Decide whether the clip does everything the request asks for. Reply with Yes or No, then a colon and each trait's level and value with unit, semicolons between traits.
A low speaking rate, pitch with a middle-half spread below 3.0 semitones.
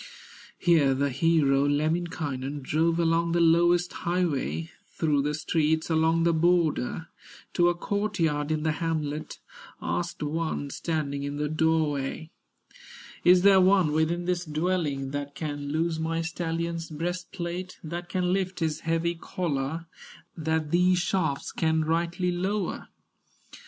Yes: slow, 130 wpm; narrow, 2.5 semitones